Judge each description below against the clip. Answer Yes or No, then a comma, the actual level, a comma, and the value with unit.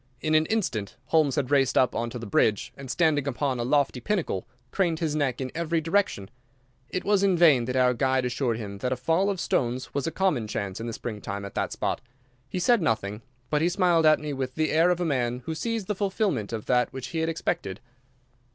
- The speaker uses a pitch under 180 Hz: Yes, medium, 140 Hz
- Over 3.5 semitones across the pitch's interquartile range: Yes, wide, 5.6 semitones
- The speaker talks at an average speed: No, fast, 235 wpm